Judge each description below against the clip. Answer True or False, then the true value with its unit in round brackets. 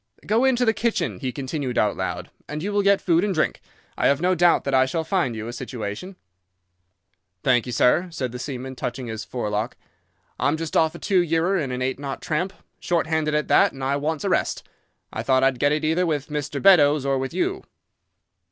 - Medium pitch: True (145 Hz)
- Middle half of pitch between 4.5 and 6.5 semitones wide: True (5.1 semitones)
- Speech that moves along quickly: True (215 wpm)